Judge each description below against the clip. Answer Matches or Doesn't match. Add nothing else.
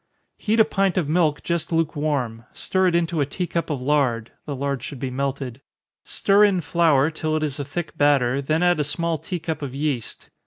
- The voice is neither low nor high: Matches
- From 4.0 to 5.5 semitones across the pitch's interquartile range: Doesn't match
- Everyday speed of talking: Doesn't match